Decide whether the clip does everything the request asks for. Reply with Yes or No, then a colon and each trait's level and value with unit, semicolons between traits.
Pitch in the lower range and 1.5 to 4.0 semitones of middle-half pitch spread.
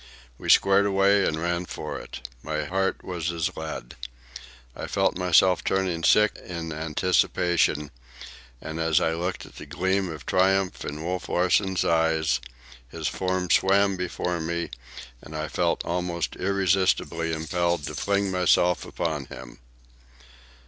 Yes: very low, 85 Hz; narrow, 2.6 semitones